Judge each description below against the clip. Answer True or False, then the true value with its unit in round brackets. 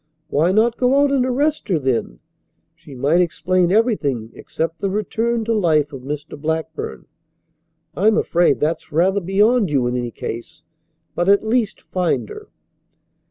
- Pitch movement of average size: False (6.8 semitones)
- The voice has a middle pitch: True (180 Hz)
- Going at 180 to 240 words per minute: False (155 wpm)